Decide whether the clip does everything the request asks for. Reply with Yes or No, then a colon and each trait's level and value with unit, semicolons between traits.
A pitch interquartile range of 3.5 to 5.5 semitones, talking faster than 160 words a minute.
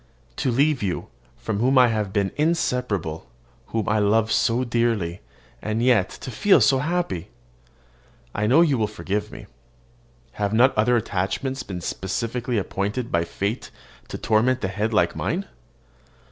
No: average, 3.9 semitones; average, 145 wpm